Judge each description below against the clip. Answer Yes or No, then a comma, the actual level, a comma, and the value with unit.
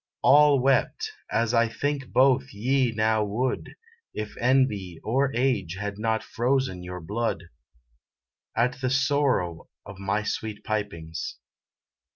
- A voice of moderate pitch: No, low, 115 Hz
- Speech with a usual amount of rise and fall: Yes, average, 4.5 semitones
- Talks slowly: Yes, slow, 125 wpm